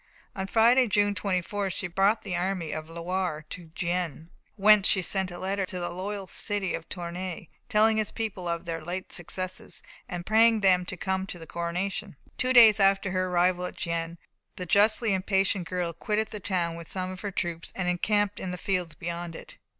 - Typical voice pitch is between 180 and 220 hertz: Yes, medium, 185 Hz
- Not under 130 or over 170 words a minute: No, average, 195 wpm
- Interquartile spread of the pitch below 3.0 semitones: Yes, narrow, 2.6 semitones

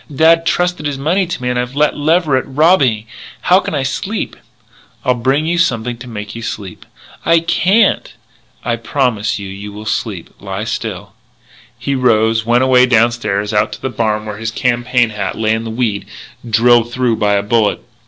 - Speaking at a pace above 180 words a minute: Yes, average, 190 wpm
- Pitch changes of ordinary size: Yes, average, 4.3 semitones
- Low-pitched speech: Yes, low, 120 Hz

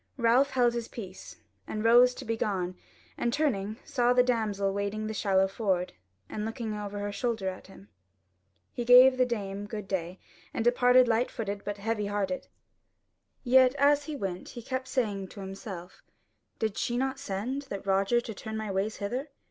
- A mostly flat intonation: No, average, 3.9 semitones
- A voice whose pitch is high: Yes, high, 220 Hz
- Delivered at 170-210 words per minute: Yes, average, 180 wpm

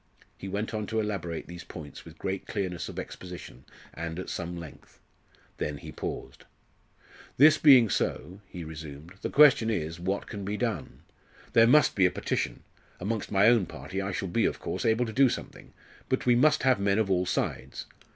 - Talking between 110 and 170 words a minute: No, average, 190 wpm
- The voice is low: Yes, low, 100 Hz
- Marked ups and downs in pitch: No, average, 4.6 semitones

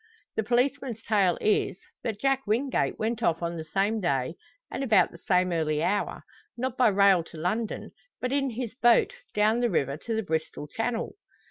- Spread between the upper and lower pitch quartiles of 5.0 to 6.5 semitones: Yes, wide, 5.6 semitones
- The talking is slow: No, average, 185 wpm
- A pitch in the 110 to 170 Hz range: No, high, 215 Hz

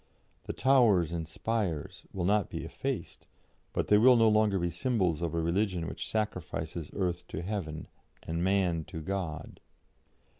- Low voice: Yes, very low, 90 Hz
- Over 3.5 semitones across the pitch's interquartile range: Yes, average, 4.2 semitones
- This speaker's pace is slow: No, average, 155 wpm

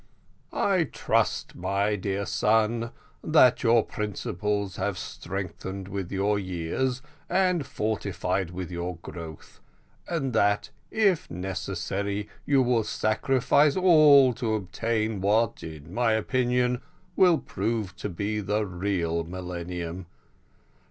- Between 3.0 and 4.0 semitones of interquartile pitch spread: No, average, 4.8 semitones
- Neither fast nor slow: No, slow, 110 wpm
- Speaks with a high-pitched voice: No, low, 105 Hz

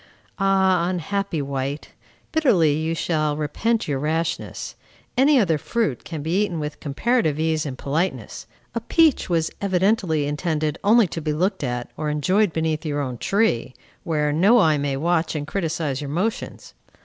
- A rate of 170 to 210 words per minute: No, average, 160 wpm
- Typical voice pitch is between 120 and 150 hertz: No, medium, 160 Hz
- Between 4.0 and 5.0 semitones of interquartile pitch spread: Yes, average, 4.7 semitones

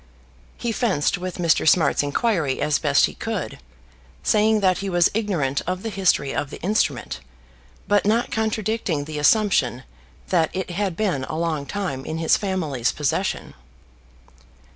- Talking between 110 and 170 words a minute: Yes, average, 150 wpm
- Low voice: No, medium, 180 Hz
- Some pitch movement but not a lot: No, wide, 5.8 semitones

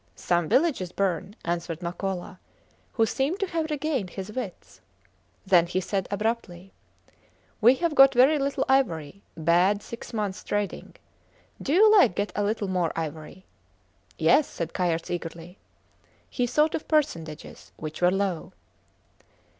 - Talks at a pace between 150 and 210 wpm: No, average, 140 wpm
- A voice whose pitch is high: Yes, high, 195 Hz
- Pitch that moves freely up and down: Yes, wide, 7.3 semitones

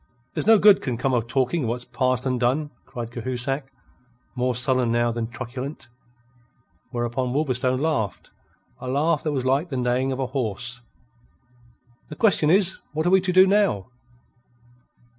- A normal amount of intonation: Yes, average, 3.8 semitones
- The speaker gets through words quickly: No, average, 160 wpm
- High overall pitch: No, low, 130 Hz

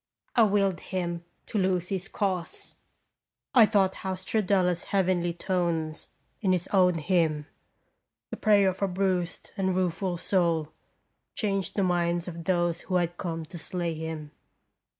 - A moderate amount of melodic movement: No, narrow, 2.1 semitones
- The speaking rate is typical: Yes, average, 145 wpm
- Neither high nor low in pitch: Yes, medium, 180 Hz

